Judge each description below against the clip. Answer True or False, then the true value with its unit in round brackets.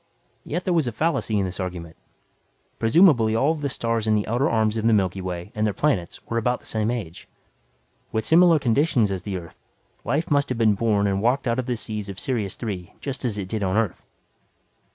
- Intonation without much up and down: False (4.4 semitones)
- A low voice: True (110 Hz)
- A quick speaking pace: True (220 wpm)